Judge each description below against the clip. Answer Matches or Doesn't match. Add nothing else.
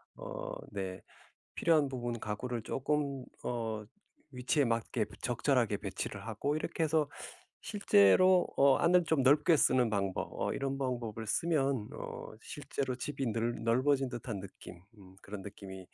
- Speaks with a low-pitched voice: Matches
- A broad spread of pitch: Doesn't match